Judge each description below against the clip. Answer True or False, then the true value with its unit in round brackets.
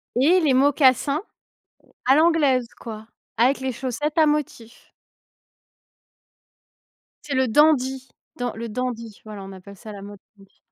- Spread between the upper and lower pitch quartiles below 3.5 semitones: False (4.5 semitones)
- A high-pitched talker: True (255 Hz)